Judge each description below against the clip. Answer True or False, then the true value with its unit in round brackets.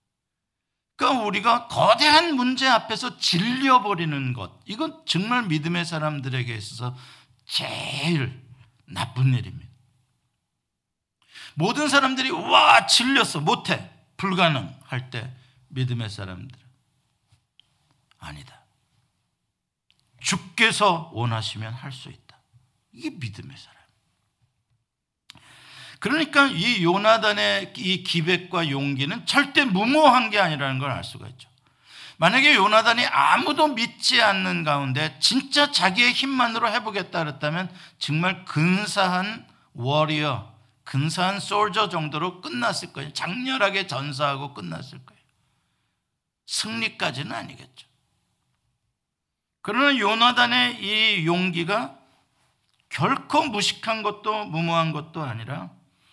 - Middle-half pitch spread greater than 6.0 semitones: True (9.0 semitones)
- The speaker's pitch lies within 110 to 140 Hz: False (170 Hz)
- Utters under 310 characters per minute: True (240 characters per minute)